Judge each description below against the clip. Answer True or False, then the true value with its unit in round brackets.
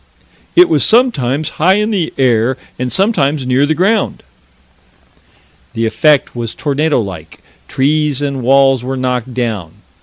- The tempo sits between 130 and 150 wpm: True (140 wpm)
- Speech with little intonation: False (4.1 semitones)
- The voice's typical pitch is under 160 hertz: True (135 Hz)